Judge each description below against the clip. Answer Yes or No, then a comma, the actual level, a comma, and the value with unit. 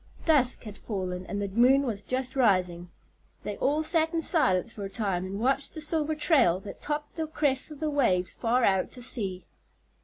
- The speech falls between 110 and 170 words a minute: No, average, 195 wpm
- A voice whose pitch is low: No, high, 245 Hz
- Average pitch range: No, wide, 7.2 semitones